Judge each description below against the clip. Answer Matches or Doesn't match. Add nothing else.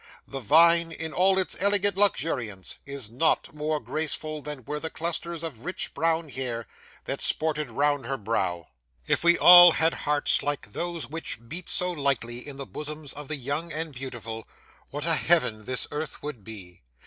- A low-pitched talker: Doesn't match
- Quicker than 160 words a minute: Matches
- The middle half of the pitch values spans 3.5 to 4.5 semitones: Matches